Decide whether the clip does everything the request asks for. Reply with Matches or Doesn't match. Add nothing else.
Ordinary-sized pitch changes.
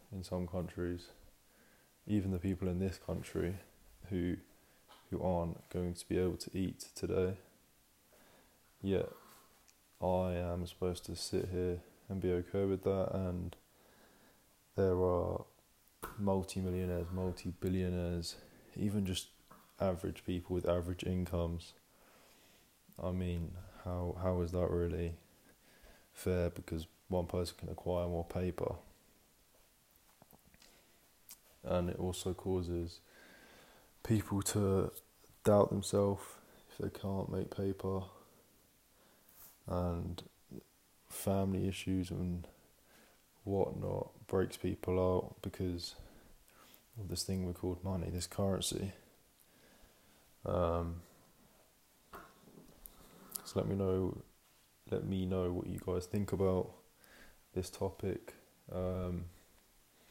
Doesn't match